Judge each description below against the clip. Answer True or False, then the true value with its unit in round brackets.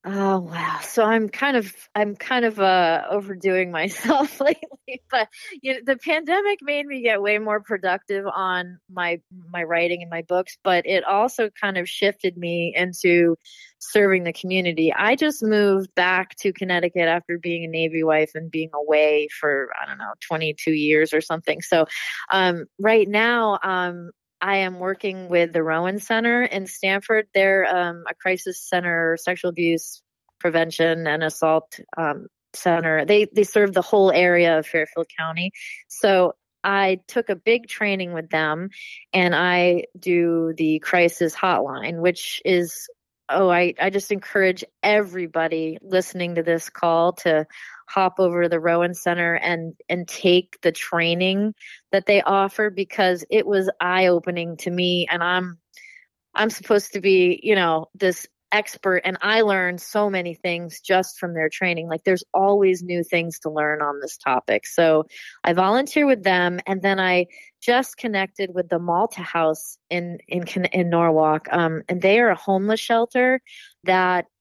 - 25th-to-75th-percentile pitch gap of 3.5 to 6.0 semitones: False (3.1 semitones)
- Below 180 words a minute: True (165 wpm)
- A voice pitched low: False (180 Hz)